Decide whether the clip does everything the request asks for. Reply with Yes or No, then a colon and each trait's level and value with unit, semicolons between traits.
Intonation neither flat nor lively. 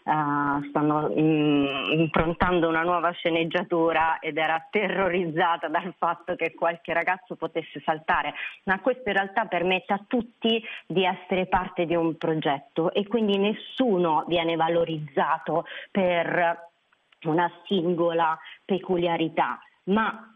No: narrow, 2.3 semitones